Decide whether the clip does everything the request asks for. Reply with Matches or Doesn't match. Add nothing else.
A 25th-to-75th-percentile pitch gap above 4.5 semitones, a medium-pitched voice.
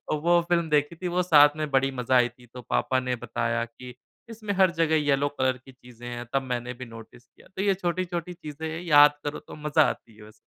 Matches